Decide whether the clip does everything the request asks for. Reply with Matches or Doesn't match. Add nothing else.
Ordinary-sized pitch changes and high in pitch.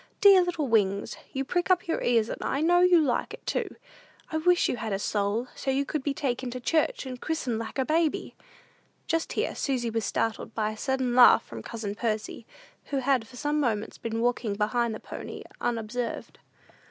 Matches